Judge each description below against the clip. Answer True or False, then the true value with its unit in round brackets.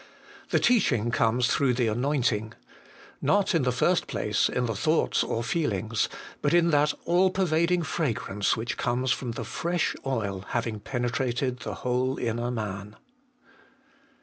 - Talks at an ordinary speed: True (145 wpm)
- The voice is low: True (125 Hz)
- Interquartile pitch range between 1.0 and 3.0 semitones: False (5.0 semitones)